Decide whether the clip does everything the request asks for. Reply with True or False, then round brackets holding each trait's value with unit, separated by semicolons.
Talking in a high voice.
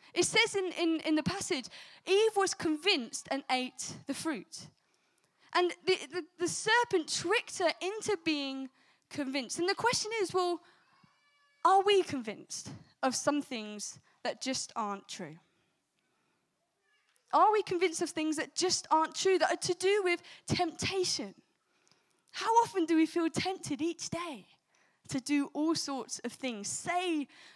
True (335 Hz)